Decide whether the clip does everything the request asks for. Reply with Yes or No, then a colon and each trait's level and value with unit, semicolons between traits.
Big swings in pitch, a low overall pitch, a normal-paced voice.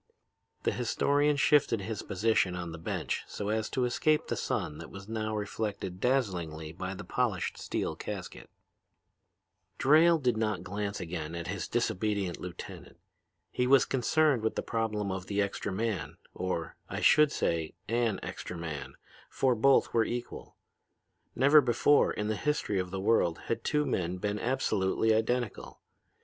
No: average, 4.9 semitones; low, 105 Hz; average, 155 wpm